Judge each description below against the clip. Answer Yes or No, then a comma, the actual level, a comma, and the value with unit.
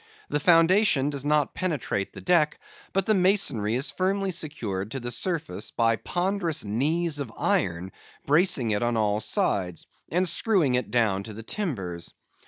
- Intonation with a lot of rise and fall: Yes, wide, 8.2 semitones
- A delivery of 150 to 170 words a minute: Yes, average, 160 wpm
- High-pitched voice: No, medium, 140 Hz